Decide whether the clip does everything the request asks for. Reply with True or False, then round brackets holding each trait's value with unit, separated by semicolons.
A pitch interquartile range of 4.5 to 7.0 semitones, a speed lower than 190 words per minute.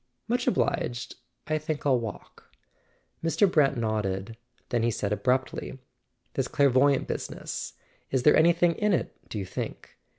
True (5.5 semitones; 140 wpm)